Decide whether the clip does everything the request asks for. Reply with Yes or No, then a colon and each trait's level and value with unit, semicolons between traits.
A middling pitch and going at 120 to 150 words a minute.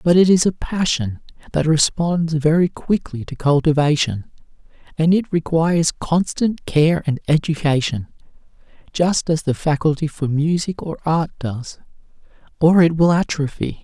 Yes: medium, 160 Hz; slow, 135 wpm